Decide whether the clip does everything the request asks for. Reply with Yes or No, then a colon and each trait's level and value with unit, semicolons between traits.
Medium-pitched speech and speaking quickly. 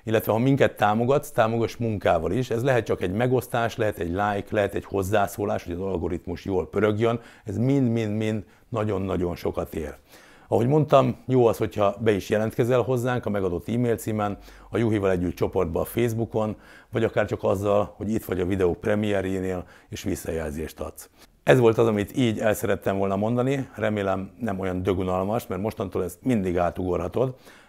No: low, 105 Hz; fast, 170 wpm